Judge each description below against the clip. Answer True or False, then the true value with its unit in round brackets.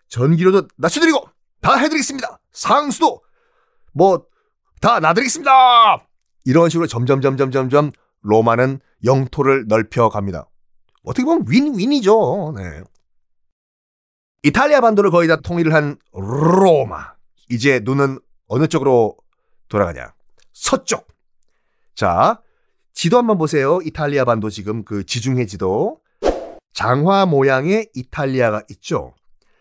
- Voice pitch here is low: False (145 Hz)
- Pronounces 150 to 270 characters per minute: True (255 characters per minute)